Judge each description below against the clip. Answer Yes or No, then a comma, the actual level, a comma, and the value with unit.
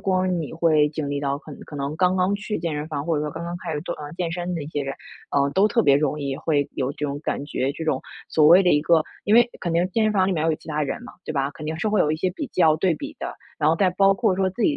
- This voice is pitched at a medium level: Yes, medium, 160 Hz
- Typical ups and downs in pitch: Yes, average, 3.9 semitones